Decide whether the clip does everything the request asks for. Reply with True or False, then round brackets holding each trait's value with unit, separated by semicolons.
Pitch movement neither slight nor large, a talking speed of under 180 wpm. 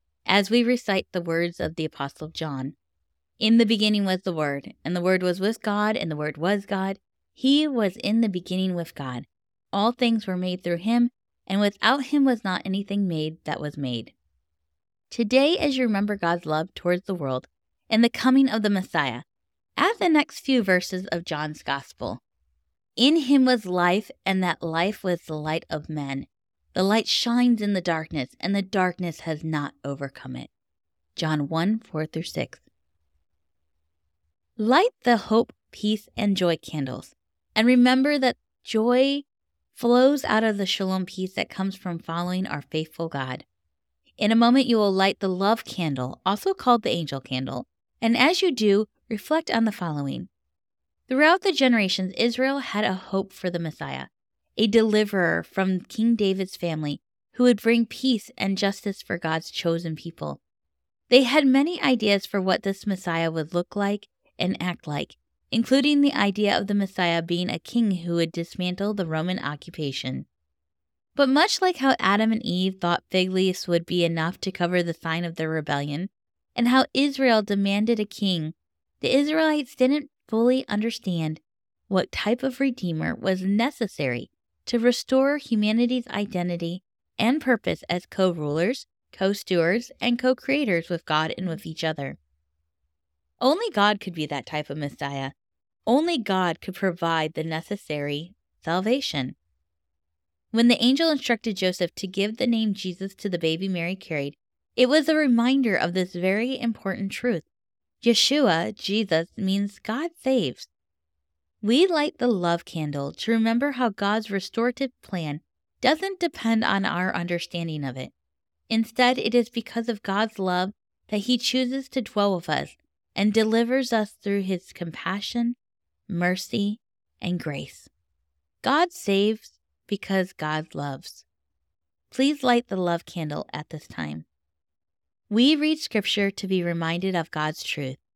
False (6.6 semitones; 160 wpm)